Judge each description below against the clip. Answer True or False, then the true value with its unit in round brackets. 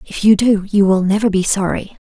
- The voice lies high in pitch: True (200 Hz)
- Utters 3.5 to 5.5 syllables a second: True (5.4 syllables/s)